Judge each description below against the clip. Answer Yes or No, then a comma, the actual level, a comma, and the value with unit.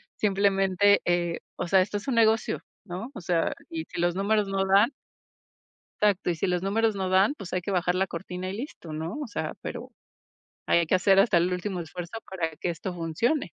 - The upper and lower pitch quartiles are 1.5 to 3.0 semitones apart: Yes, narrow, 2.6 semitones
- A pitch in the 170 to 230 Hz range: Yes, high, 190 Hz